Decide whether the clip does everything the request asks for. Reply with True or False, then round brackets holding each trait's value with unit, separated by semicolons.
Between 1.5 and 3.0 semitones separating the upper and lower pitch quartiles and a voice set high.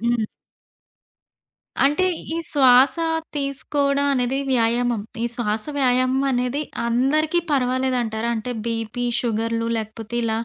True (2.7 semitones; 245 Hz)